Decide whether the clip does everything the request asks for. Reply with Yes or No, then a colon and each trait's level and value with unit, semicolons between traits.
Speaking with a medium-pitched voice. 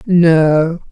Yes: medium, 165 Hz